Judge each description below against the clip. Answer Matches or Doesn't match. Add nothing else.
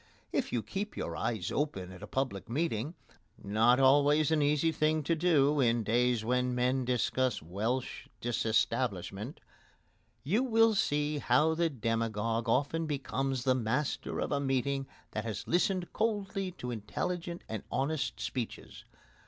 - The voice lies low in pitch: Matches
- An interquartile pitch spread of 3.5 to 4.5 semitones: Doesn't match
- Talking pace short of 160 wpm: Matches